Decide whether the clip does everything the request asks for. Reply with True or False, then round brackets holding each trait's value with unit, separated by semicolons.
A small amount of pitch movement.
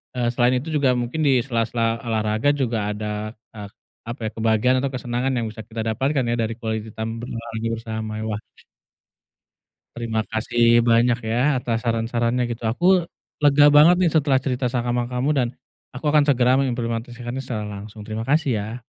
True (2.3 semitones)